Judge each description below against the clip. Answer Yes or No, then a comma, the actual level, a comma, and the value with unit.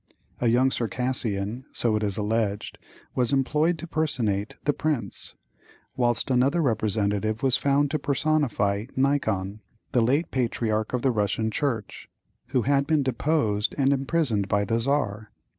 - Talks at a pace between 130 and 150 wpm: Yes, average, 140 wpm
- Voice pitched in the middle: No, low, 120 Hz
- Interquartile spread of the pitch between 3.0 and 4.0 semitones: No, average, 4.6 semitones